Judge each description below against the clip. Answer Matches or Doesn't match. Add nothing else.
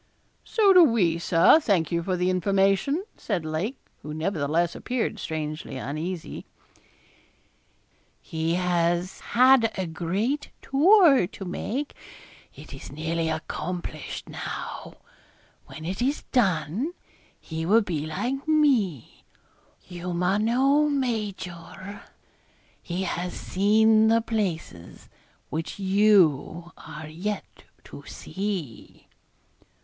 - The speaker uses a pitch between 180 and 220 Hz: Matches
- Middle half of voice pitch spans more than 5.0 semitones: Matches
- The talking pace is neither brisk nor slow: Doesn't match